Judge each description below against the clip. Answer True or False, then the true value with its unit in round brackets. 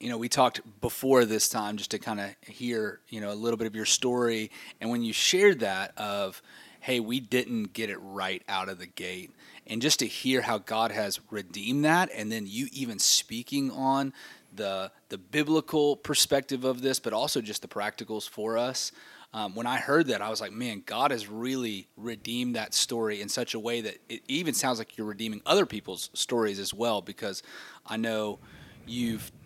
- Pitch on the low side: True (115 Hz)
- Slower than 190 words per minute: False (200 wpm)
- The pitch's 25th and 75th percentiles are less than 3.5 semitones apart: True (3.0 semitones)